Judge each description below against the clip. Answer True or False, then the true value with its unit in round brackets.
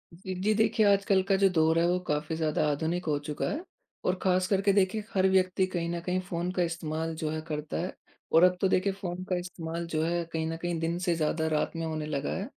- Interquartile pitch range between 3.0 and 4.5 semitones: False (2.6 semitones)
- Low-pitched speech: False (175 Hz)